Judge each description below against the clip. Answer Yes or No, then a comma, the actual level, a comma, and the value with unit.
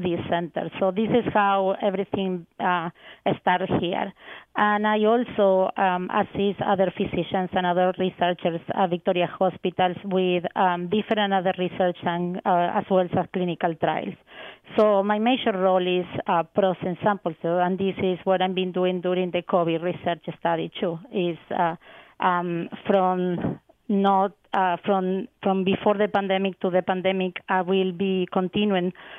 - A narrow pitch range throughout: Yes, narrow, 1.7 semitones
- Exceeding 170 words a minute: No, average, 150 wpm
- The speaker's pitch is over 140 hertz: Yes, medium, 185 Hz